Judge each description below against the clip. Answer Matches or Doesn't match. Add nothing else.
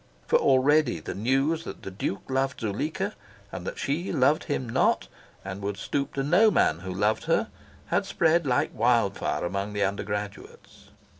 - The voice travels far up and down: Matches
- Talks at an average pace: Matches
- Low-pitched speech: Matches